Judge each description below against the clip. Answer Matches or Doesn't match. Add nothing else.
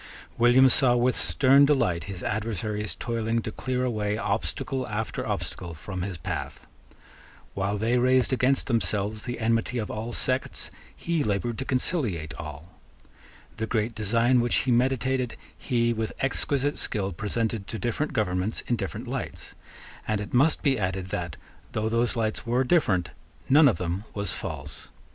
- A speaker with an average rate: Matches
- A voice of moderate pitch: Doesn't match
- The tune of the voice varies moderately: Matches